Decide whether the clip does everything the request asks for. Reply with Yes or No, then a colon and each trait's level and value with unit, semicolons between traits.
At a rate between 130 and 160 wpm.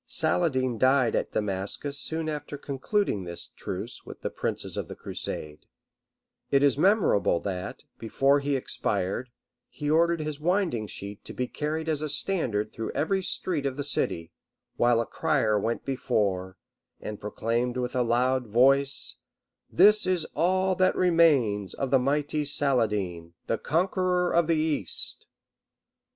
Yes: average, 150 wpm